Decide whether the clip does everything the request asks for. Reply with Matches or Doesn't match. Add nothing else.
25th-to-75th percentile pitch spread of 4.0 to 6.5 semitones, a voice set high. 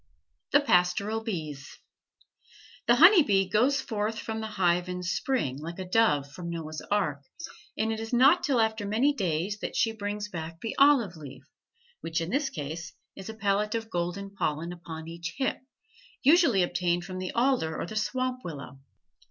Matches